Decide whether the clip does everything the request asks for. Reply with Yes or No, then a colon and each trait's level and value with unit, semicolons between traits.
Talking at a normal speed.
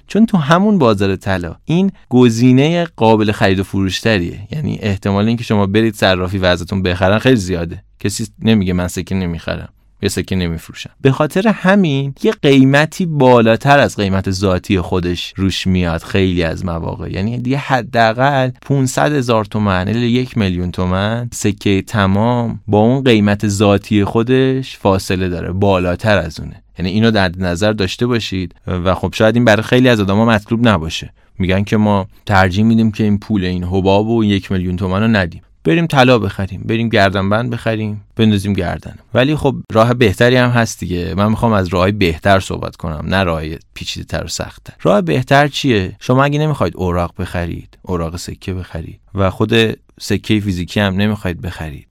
No: fast, 170 wpm